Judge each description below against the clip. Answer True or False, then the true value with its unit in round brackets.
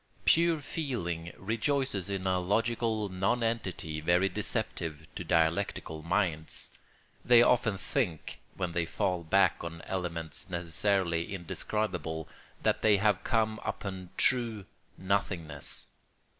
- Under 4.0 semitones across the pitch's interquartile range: False (4.7 semitones)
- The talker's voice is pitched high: False (95 Hz)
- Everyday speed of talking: False (110 wpm)